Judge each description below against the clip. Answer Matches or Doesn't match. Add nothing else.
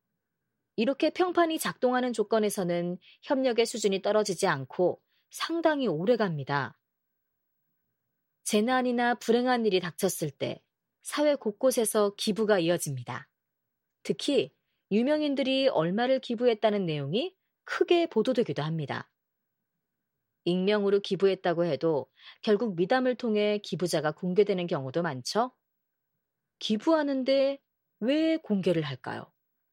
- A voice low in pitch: Doesn't match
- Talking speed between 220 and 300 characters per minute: Matches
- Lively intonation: Matches